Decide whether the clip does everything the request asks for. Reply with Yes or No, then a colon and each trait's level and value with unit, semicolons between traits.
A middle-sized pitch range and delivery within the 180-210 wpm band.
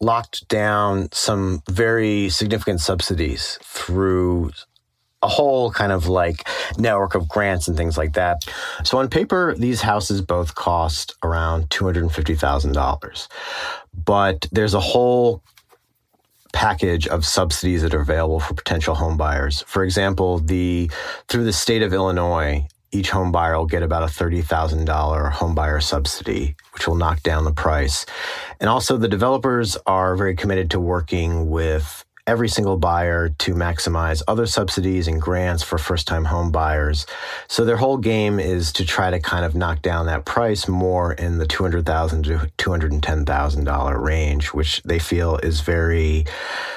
No: average, 3.2 semitones; average, 150 wpm